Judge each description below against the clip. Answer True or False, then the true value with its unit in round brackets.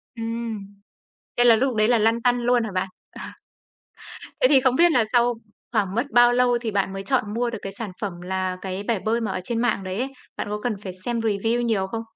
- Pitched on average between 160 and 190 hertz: False (230 Hz)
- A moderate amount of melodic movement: True (3.3 semitones)